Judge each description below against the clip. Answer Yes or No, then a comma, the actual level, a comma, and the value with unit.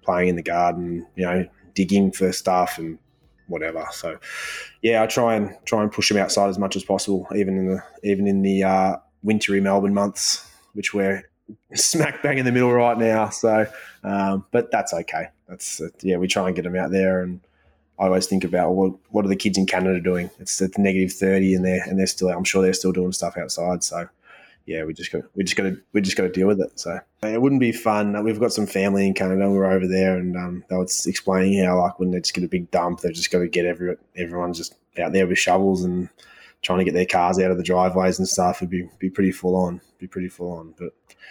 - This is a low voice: Yes, very low, 95 Hz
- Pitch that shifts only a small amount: Yes, narrow, 1.6 semitones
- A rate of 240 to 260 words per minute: Yes, fast, 250 wpm